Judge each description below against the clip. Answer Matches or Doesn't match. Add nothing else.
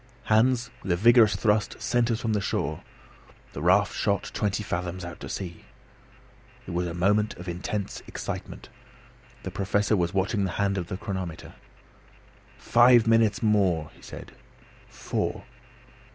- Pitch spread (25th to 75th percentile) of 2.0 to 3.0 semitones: Doesn't match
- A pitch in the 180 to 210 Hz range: Doesn't match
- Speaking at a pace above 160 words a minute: Doesn't match